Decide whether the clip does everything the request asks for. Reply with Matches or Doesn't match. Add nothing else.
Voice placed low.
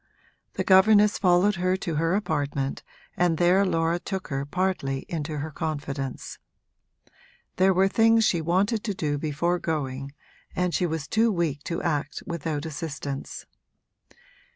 Doesn't match